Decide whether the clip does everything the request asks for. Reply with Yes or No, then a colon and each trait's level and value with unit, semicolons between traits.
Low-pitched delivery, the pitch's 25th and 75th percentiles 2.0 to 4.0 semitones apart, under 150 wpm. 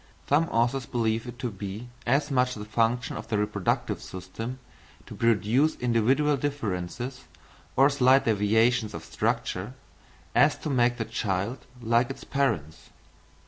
Yes: low, 120 Hz; average, 3.5 semitones; average, 140 wpm